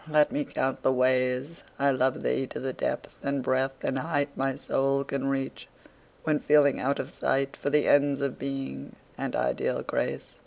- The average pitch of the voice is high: No, low, 135 Hz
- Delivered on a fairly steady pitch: Yes, narrow, 1.4 semitones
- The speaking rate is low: No, average, 185 wpm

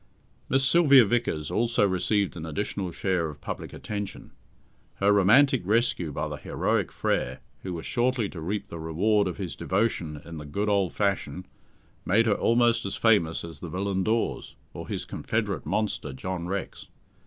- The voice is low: Yes, low, 100 Hz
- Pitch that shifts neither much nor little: Yes, average, 4.6 semitones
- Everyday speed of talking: Yes, average, 165 wpm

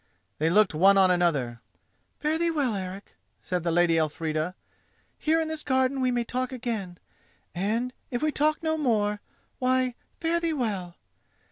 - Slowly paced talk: No, average, 155 wpm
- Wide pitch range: Yes, wide, 7.6 semitones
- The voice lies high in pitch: Yes, high, 225 Hz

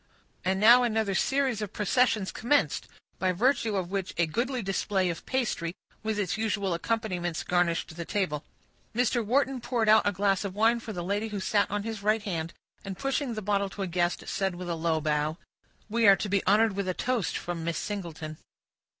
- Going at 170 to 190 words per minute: No, average, 200 wpm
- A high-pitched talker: Yes, high, 200 Hz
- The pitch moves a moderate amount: Yes, average, 3.9 semitones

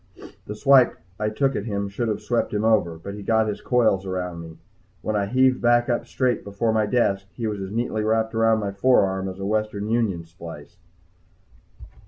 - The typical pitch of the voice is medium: No, low, 105 Hz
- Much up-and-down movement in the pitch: No, average, 3.0 semitones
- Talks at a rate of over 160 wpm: Yes, average, 200 wpm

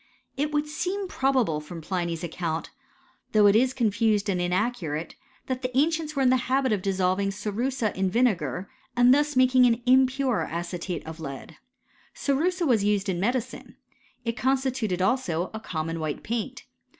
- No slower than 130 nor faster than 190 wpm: Yes, average, 165 wpm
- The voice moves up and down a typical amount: No, wide, 6.2 semitones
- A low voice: No, high, 225 Hz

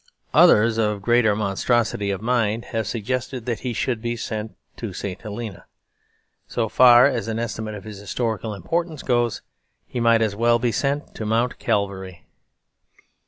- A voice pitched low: Yes, low, 115 Hz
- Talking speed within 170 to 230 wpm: No, average, 160 wpm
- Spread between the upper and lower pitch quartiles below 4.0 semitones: Yes, narrow, 2.4 semitones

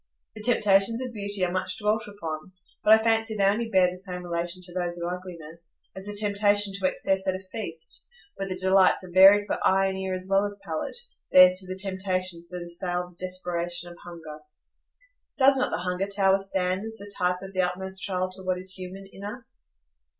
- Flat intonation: Yes, narrow, 1.9 semitones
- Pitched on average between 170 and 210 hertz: Yes, high, 190 Hz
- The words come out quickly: Yes, fast, 210 wpm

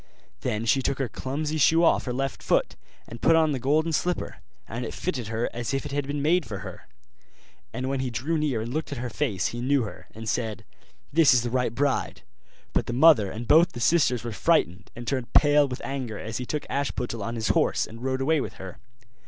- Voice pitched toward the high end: No, low, 130 Hz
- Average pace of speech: No, fast, 230 wpm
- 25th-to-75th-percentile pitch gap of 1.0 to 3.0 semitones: No, average, 4.0 semitones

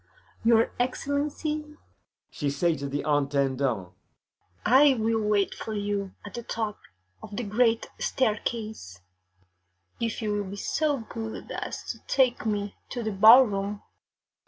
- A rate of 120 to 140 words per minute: Yes, slow, 135 wpm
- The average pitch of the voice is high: Yes, high, 215 Hz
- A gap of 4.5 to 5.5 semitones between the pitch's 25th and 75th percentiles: No, average, 3.4 semitones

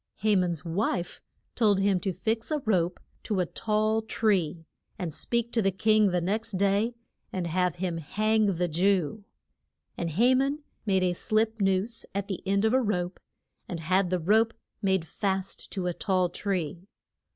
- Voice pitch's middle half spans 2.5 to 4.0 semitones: Yes, average, 3.3 semitones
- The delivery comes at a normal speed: Yes, average, 175 wpm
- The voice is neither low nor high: No, high, 195 Hz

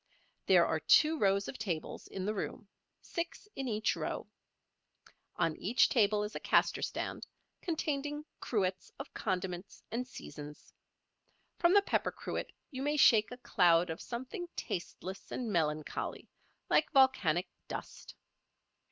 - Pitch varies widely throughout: Yes, wide, 6.8 semitones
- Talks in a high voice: Yes, high, 215 Hz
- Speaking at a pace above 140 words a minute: No, slow, 135 wpm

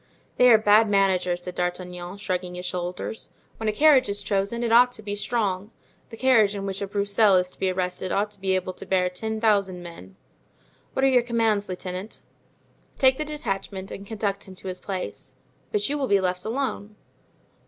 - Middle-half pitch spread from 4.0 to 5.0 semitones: No, average, 3.2 semitones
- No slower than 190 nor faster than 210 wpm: Yes, average, 195 wpm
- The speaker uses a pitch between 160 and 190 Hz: No, high, 200 Hz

